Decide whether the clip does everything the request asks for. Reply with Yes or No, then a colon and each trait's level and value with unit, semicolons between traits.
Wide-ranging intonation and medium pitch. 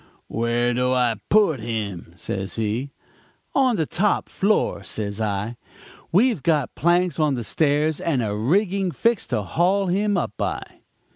Yes: wide, 8.7 semitones; medium, 145 Hz